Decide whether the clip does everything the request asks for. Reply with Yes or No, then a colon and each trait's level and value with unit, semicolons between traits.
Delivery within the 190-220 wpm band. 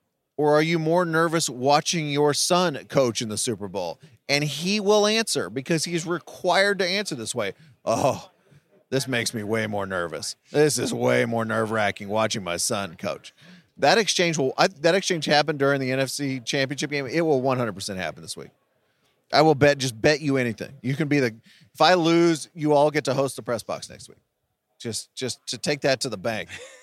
Yes: average, 200 wpm